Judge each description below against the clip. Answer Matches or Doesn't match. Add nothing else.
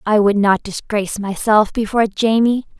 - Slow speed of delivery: Doesn't match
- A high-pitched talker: Matches